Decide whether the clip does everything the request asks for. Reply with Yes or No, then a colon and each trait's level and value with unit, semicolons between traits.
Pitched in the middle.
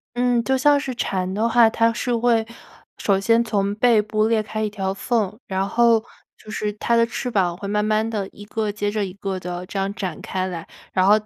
No: high, 215 Hz